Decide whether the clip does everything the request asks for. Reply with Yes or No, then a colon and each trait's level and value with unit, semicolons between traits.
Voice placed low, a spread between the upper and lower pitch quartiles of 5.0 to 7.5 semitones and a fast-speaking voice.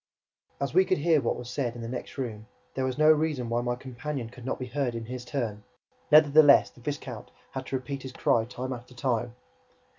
No: low, 130 Hz; average, 2.9 semitones; fast, 215 wpm